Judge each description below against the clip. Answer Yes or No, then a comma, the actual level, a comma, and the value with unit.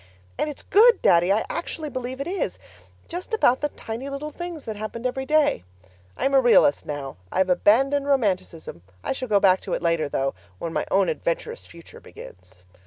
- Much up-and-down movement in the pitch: Yes, wide, 8.5 semitones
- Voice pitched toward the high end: Yes, high, 245 Hz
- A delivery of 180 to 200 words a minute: Yes, average, 185 wpm